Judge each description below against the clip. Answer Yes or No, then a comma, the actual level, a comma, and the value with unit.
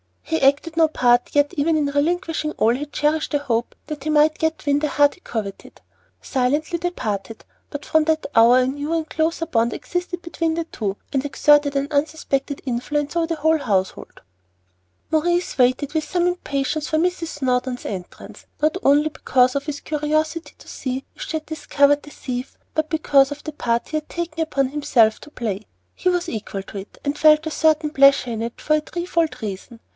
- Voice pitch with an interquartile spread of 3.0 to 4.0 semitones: Yes, average, 3.5 semitones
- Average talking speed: Yes, average, 195 wpm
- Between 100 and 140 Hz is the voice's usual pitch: No, very high, 295 Hz